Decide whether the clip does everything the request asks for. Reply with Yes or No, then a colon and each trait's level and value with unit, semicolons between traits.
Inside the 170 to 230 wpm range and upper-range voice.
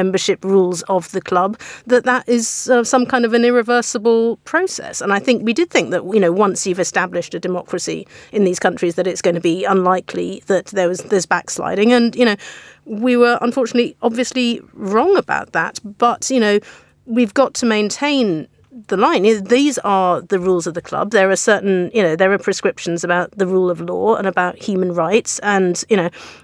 Yes: average, 200 wpm; high, 200 Hz